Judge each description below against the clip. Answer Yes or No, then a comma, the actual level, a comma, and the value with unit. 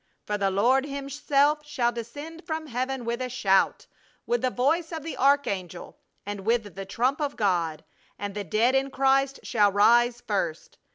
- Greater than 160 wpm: Yes, average, 170 wpm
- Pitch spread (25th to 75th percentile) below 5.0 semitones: No, wide, 5.4 semitones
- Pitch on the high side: Yes, high, 245 Hz